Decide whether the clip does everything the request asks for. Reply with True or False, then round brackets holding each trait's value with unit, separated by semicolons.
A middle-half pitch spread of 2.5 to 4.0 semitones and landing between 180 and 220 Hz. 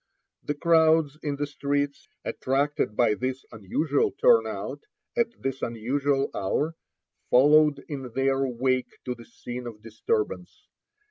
False (3.4 semitones; 140 Hz)